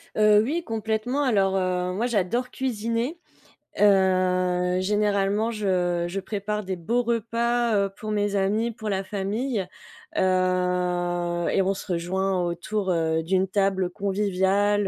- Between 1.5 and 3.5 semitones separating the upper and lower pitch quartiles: Yes, average, 2.8 semitones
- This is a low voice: No, high, 195 Hz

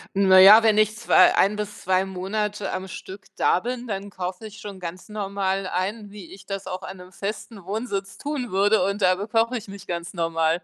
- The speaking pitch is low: No, high, 195 Hz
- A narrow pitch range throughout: Yes, narrow, 2.2 semitones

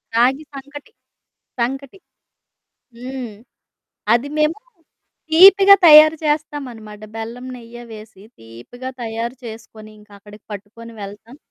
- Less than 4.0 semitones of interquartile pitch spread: No, average, 4.7 semitones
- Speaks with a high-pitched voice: Yes, high, 240 Hz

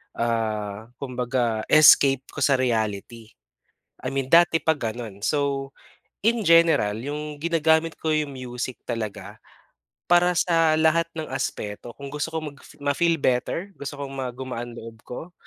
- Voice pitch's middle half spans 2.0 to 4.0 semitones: No, average, 5.0 semitones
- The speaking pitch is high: No, low, 135 Hz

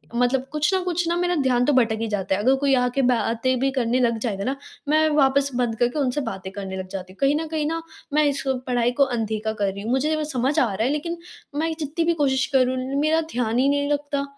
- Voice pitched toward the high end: Yes, very high, 260 Hz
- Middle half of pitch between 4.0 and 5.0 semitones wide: Yes, average, 4.4 semitones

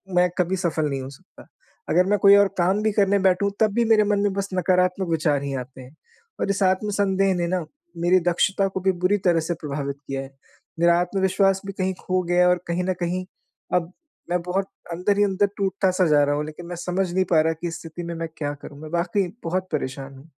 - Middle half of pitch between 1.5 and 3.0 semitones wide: Yes, average, 2.7 semitones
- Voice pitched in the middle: Yes, medium, 180 Hz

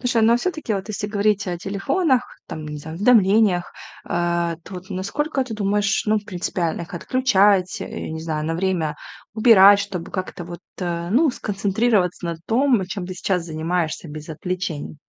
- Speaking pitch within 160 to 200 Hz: Yes, high, 190 Hz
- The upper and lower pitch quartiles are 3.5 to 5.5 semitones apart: Yes, average, 3.8 semitones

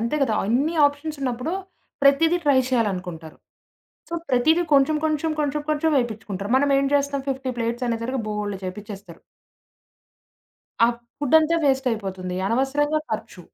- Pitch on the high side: Yes, very high, 260 Hz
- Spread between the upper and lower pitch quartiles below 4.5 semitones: No, average, 5.3 semitones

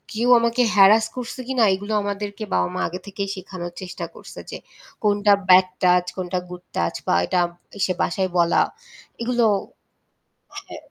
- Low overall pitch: No, high, 195 Hz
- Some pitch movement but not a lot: Yes, average, 3.1 semitones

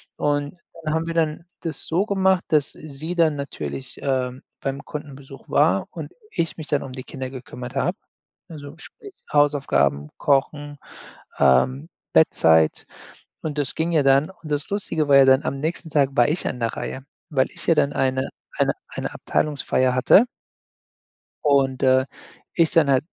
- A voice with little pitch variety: No, average, 3.1 semitones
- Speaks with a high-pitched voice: No, medium, 145 Hz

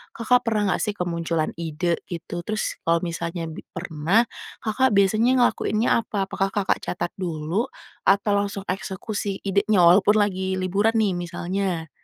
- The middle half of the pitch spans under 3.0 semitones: No, average, 3.4 semitones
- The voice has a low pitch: No, high, 195 Hz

